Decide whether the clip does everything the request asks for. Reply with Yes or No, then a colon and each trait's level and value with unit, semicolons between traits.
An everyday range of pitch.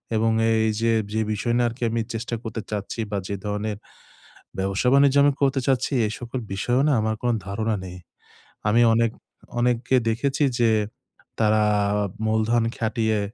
No: narrow, 2.1 semitones